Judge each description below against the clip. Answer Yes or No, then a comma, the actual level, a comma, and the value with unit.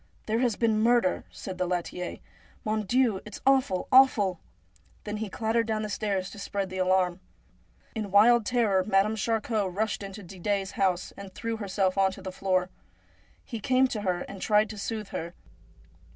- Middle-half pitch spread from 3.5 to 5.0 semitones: No, average, 2.8 semitones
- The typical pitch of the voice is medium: No, high, 205 Hz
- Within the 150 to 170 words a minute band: No, average, 190 wpm